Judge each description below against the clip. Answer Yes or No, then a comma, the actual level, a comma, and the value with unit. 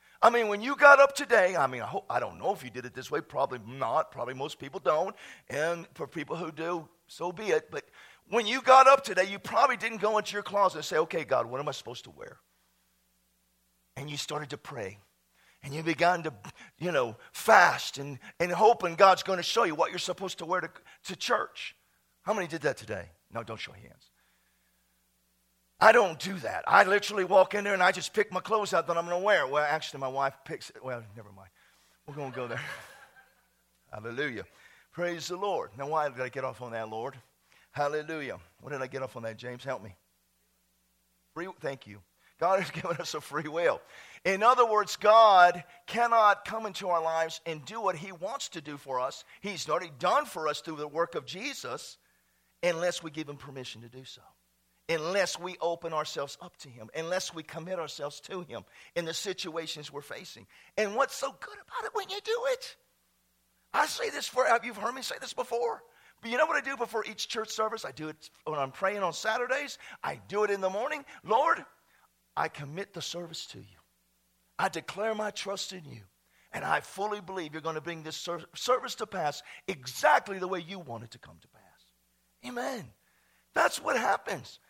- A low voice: No, medium, 170 Hz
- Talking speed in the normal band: No, fast, 215 wpm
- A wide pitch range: Yes, wide, 7.7 semitones